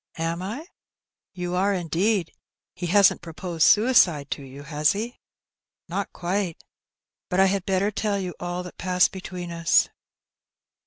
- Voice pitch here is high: No, medium, 180 Hz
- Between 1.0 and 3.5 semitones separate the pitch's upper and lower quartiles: Yes, average, 2.8 semitones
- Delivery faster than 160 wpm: No, average, 145 wpm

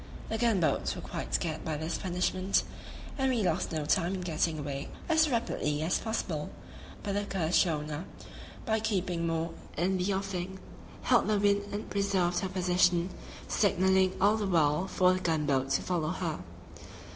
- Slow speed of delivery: No, average, 170 wpm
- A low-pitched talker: No, medium, 180 Hz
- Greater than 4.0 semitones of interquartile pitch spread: No, average, 3.6 semitones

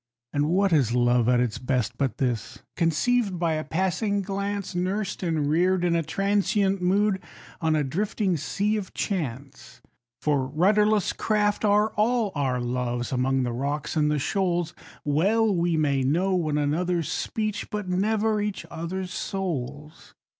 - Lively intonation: Yes, wide, 5.8 semitones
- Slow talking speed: No, average, 155 wpm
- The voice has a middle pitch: Yes, medium, 175 Hz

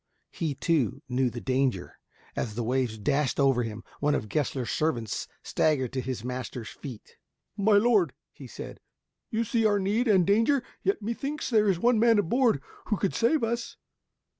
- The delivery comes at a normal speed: Yes, average, 175 wpm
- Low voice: No, medium, 155 Hz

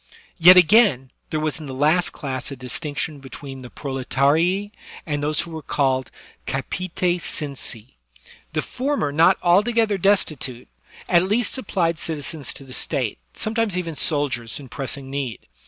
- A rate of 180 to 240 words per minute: No, average, 150 wpm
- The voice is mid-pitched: Yes, medium, 155 Hz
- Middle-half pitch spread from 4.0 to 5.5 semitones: Yes, average, 5.2 semitones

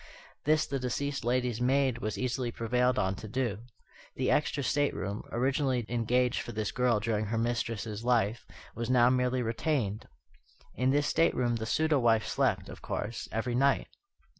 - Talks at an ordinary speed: Yes, average, 160 wpm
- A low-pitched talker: Yes, low, 120 Hz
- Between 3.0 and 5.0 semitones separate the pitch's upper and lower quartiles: No, narrow, 2.4 semitones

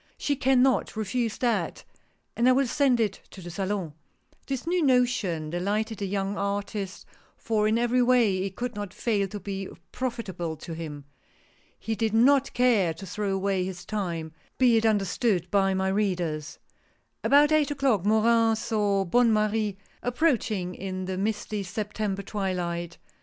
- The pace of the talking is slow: No, average, 165 wpm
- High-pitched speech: Yes, high, 210 Hz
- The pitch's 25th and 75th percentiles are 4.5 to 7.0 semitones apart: No, average, 3.9 semitones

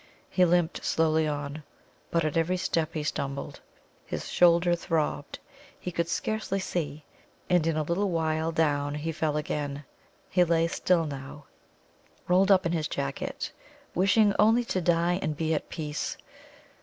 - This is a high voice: No, medium, 165 Hz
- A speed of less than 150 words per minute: No, average, 155 wpm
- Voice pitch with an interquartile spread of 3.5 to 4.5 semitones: No, average, 2.8 semitones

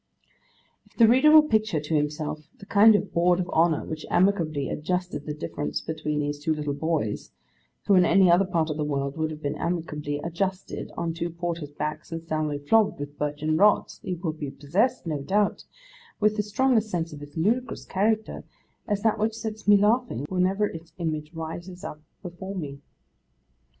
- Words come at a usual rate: Yes, average, 185 wpm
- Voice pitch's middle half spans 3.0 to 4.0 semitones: No, average, 4.9 semitones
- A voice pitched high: No, medium, 170 Hz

